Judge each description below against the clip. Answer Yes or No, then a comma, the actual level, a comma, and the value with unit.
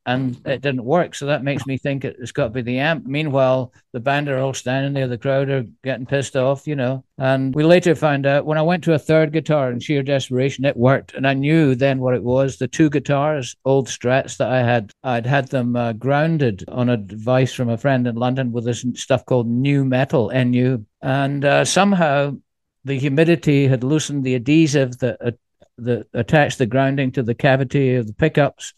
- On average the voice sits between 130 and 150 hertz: Yes, low, 135 Hz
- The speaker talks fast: Yes, fast, 215 wpm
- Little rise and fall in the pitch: Yes, narrow, 2.2 semitones